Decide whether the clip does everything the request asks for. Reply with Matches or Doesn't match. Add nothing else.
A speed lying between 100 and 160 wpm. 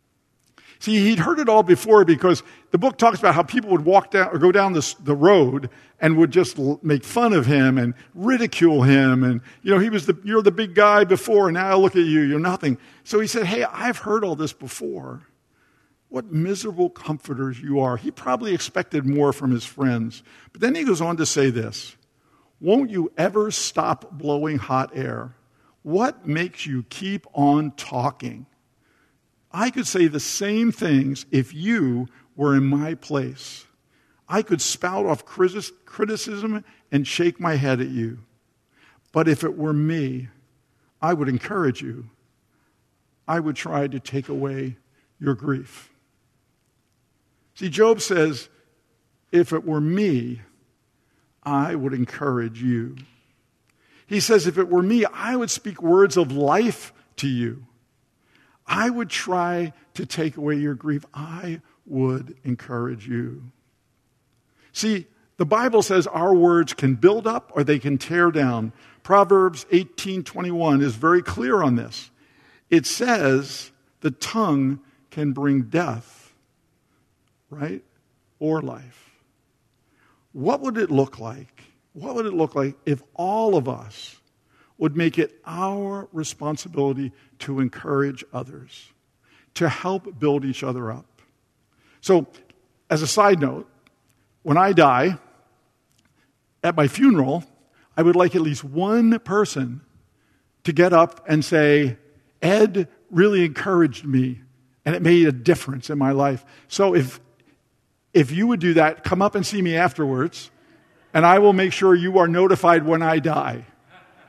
Matches